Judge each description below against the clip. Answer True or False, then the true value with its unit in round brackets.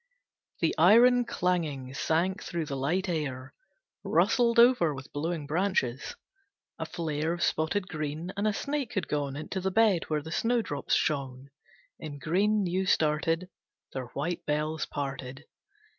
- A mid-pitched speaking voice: True (160 Hz)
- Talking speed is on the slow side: False (145 wpm)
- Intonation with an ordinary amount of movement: True (4.6 semitones)